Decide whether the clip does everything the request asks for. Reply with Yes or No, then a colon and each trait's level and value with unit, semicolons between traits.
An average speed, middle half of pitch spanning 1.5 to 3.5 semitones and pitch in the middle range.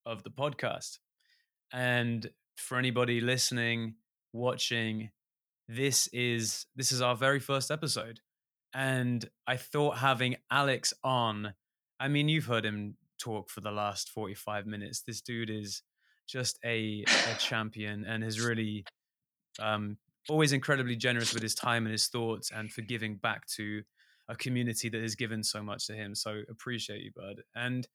No: average, 150 wpm; narrow, 2.6 semitones; low, 115 Hz